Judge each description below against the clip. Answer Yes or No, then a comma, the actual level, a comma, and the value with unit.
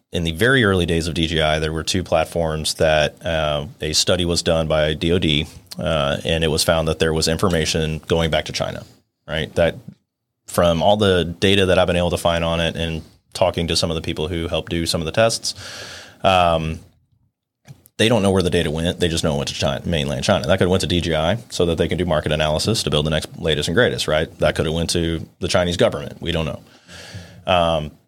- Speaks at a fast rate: Yes, fast, 235 wpm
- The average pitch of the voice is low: Yes, very low, 85 Hz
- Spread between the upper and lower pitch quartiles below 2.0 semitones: No, narrow, 2.5 semitones